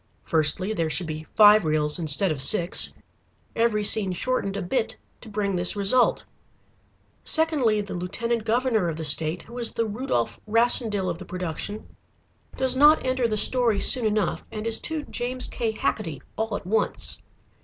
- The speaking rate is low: No, average, 165 wpm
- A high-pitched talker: Yes, high, 210 Hz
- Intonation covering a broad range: No, average, 4.9 semitones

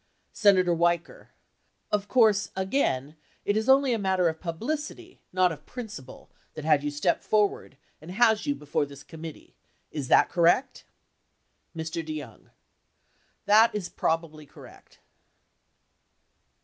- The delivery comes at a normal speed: No, slow, 125 wpm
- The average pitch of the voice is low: No, medium, 180 Hz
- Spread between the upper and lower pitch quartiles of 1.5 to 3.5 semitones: No, wide, 5.6 semitones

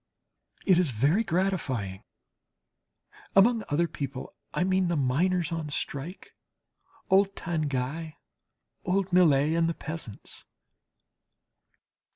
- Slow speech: Yes, slow, 100 wpm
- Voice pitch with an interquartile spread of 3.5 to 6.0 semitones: Yes, average, 4.6 semitones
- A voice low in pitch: No, medium, 165 Hz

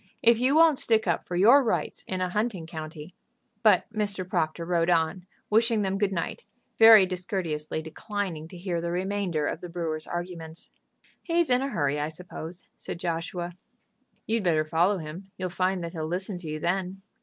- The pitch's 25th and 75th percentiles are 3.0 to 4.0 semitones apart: Yes, average, 3.6 semitones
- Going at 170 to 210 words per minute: Yes, average, 185 wpm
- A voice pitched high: No, medium, 180 Hz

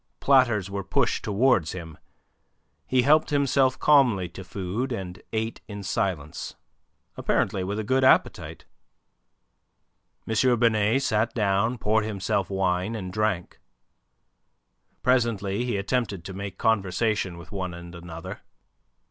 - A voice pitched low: Yes, low, 105 Hz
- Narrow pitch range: No, average, 4.2 semitones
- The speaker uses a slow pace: Yes, slow, 120 wpm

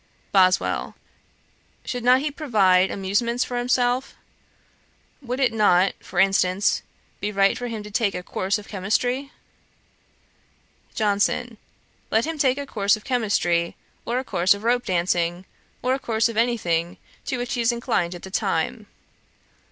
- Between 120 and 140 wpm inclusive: No, average, 155 wpm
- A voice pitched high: Yes, high, 220 Hz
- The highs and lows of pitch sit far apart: No, average, 4.4 semitones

